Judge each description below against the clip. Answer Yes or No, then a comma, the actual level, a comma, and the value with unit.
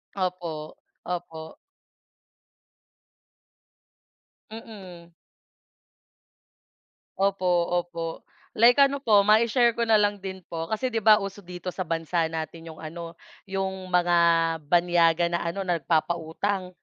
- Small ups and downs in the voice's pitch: No, average, 3.4 semitones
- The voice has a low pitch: No, medium, 180 Hz